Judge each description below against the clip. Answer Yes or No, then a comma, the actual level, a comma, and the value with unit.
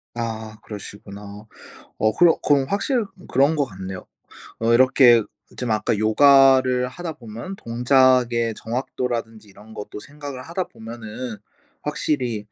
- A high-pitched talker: No, low, 120 Hz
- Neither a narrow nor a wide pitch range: Yes, average, 3.7 semitones